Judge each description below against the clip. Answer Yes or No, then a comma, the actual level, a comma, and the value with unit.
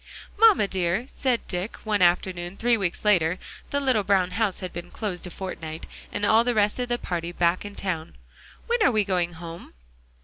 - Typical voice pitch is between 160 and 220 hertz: Yes, high, 190 Hz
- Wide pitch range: No, average, 4.1 semitones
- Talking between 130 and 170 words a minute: No, average, 195 wpm